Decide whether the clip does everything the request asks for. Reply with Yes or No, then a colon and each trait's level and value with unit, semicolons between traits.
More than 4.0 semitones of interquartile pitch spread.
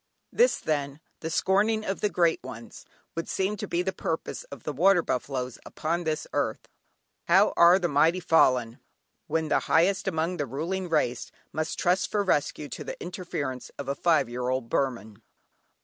Yes: average, 5.0 semitones